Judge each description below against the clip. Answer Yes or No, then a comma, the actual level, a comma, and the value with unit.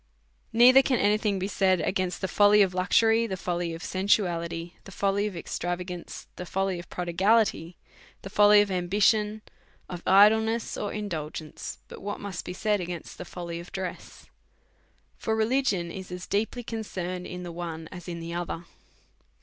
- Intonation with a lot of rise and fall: No, average, 3.0 semitones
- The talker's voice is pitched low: No, high, 190 Hz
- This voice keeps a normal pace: Yes, average, 175 wpm